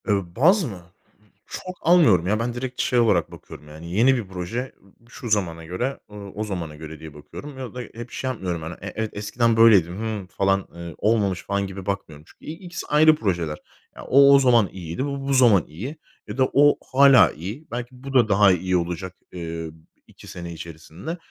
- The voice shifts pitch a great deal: Yes, wide, 6.6 semitones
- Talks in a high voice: No, low, 105 Hz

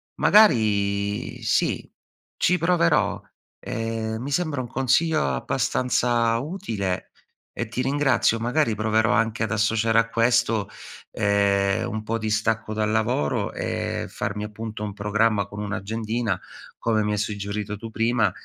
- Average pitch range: No, narrow, 2.2 semitones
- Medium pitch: No, low, 110 Hz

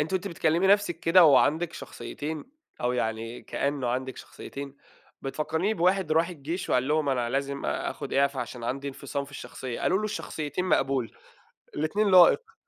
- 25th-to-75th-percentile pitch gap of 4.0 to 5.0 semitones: Yes, average, 4.4 semitones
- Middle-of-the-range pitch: Yes, medium, 145 Hz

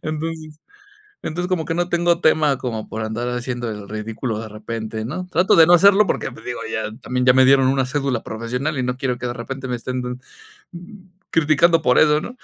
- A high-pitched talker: No, low, 130 Hz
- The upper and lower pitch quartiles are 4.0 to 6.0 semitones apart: Yes, average, 4.8 semitones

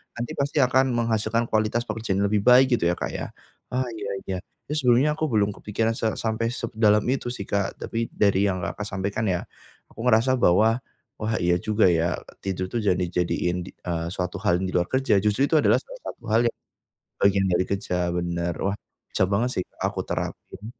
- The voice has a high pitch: No, low, 105 Hz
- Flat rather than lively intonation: No, average, 4.0 semitones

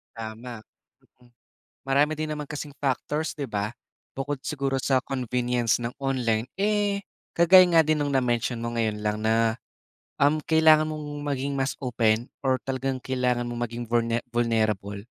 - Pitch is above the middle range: No, low, 130 Hz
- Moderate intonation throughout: Yes, average, 3.8 semitones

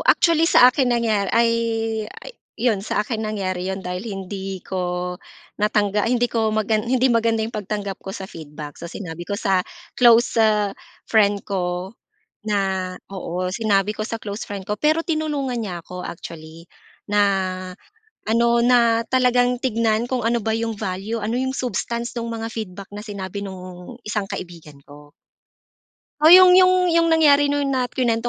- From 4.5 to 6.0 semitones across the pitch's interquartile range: No, average, 4.0 semitones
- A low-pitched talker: No, high, 215 Hz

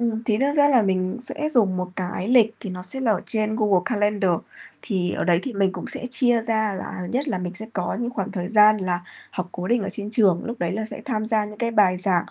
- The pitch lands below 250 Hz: Yes, high, 210 Hz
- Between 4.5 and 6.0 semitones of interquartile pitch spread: No, average, 3.9 semitones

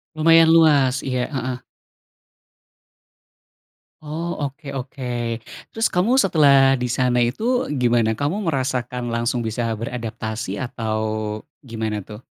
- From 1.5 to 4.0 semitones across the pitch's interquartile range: No, average, 4.5 semitones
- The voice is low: Yes, low, 130 Hz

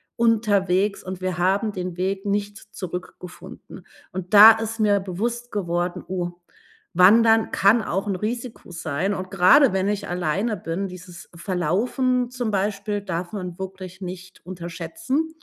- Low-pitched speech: No, high, 190 Hz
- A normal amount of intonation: Yes, average, 3.0 semitones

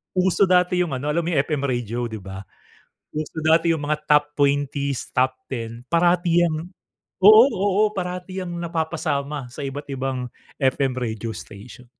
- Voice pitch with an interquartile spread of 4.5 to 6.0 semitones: Yes, average, 4.9 semitones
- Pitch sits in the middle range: Yes, medium, 150 Hz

